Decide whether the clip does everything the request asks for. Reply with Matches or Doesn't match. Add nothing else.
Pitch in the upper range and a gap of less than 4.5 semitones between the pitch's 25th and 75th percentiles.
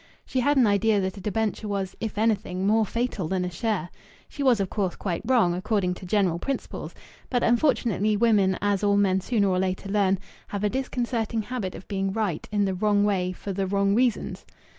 Matches